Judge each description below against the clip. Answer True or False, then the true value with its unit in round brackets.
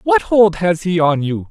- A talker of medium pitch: True (180 Hz)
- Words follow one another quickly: True (240 wpm)